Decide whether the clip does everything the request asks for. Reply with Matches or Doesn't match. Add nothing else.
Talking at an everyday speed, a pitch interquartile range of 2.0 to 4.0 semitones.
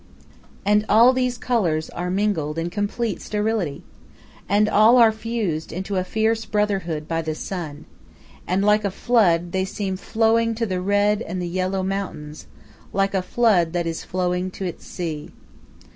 Matches